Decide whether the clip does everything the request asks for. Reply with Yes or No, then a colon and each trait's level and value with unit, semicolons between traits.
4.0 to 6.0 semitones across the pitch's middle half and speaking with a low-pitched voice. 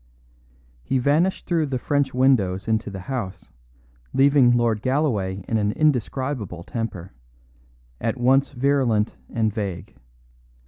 Yes: average, 4.8 semitones; low, 120 Hz